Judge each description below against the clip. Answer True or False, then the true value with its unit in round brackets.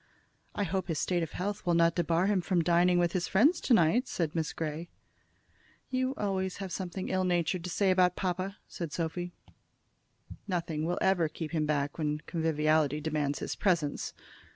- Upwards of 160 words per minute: True (175 wpm)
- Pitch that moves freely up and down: False (2.8 semitones)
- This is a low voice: False (175 Hz)